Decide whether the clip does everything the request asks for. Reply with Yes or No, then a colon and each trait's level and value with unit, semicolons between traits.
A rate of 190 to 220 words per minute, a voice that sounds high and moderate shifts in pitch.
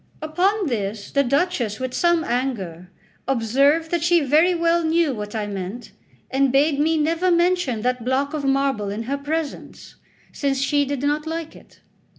No: average, 165 wpm; very high, 280 Hz; average, 4.9 semitones